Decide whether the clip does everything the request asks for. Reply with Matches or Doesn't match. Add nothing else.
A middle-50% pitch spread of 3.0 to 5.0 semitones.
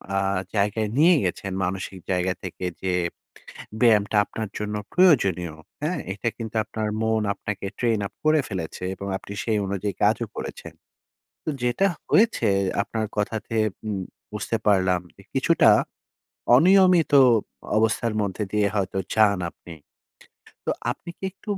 Matches